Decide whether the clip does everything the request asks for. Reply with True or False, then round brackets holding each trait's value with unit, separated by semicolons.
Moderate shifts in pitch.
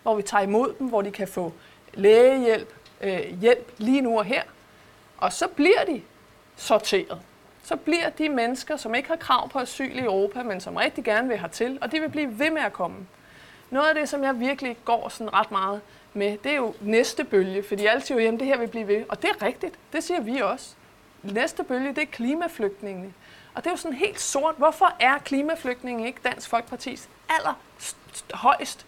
False (5.8 semitones)